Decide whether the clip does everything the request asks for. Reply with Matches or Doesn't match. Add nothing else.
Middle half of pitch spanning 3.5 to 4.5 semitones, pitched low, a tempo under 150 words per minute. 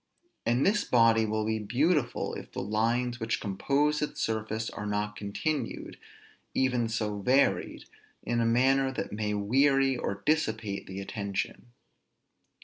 Matches